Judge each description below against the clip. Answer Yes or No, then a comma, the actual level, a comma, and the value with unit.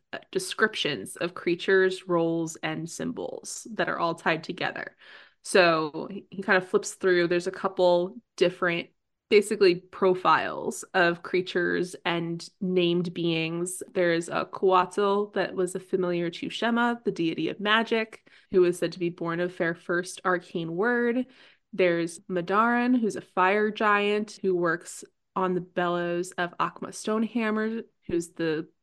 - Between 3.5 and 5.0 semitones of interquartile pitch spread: No, average, 3.0 semitones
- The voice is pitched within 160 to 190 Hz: Yes, medium, 185 Hz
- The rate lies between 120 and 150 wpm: Yes, average, 140 wpm